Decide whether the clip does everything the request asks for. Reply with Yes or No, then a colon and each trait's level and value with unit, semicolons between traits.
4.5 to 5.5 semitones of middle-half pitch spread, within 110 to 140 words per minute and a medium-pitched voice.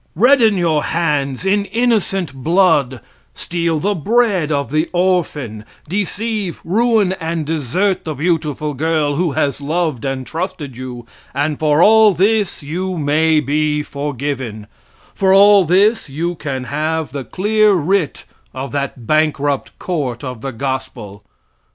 Yes: average, 5.0 semitones; slow, 135 wpm; medium, 155 Hz